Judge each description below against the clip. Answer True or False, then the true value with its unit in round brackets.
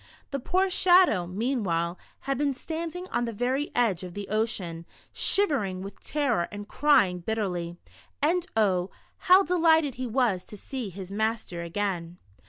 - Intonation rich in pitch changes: True (7.7 semitones)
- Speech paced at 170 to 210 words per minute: False (150 wpm)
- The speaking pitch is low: False (220 Hz)